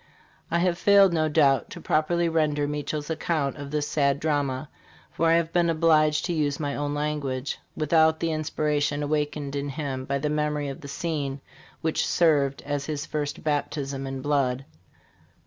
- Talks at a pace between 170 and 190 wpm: Yes, average, 175 wpm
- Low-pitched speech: No, medium, 150 Hz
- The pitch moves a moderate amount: No, narrow, 2.0 semitones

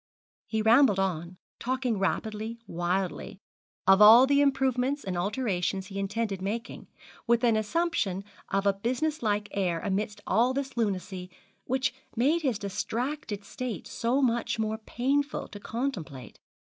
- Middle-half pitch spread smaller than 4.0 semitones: No, average, 4.7 semitones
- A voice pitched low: No, high, 220 Hz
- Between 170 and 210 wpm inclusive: No, average, 140 wpm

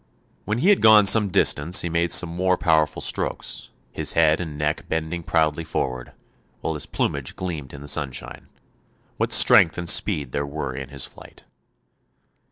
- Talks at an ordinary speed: Yes, average, 170 wpm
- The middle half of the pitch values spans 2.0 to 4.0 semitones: Yes, average, 3.5 semitones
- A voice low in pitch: Yes, very low, 80 Hz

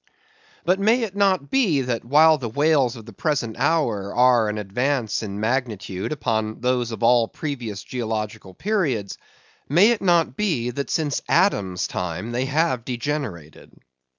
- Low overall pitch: Yes, low, 125 Hz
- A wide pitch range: Yes, wide, 6.1 semitones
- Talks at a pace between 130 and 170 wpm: Yes, average, 150 wpm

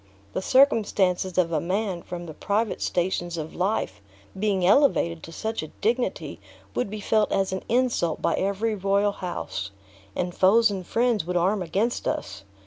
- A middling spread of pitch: Yes, average, 3.7 semitones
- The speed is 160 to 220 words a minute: Yes, average, 165 wpm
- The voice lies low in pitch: No, high, 190 Hz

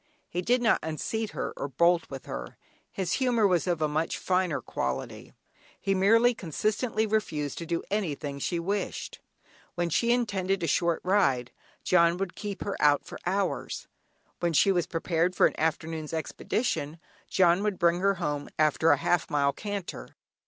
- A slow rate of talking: No, average, 165 wpm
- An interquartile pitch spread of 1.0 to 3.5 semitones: No, average, 4.1 semitones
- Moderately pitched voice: Yes, medium, 175 Hz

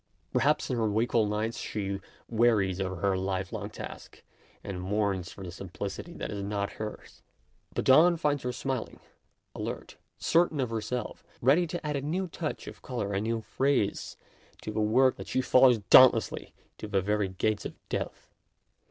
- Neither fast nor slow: Yes, average, 175 wpm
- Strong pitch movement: No, average, 4.6 semitones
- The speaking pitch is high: No, low, 110 Hz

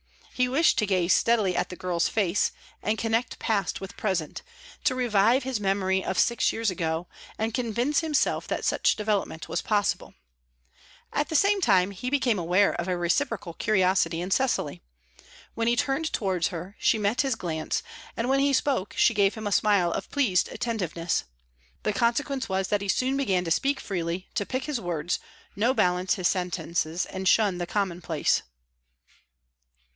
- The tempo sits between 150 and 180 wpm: Yes, average, 170 wpm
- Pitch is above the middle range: Yes, high, 200 Hz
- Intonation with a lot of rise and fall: No, average, 5.0 semitones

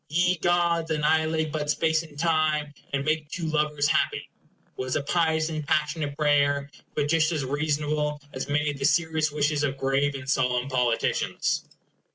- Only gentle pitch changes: Yes, narrow, 1.7 semitones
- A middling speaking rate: Yes, average, 165 wpm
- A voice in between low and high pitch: Yes, medium, 150 Hz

